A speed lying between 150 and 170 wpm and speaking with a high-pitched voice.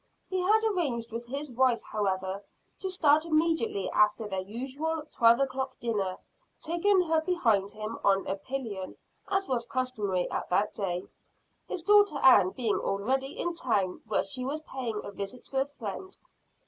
Yes: average, 160 wpm; very high, 250 Hz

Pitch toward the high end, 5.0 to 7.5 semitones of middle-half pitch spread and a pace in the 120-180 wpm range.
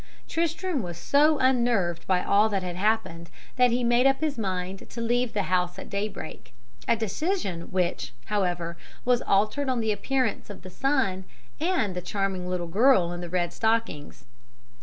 Yes: high, 205 Hz; wide, 5.6 semitones; average, 170 wpm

